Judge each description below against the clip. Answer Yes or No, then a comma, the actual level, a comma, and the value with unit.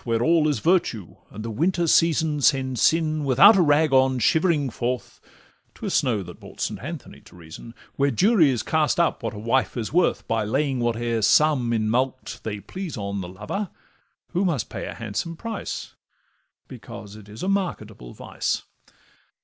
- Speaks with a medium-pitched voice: No, low, 130 Hz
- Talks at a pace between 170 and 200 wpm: Yes, average, 175 wpm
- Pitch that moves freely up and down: Yes, wide, 6.4 semitones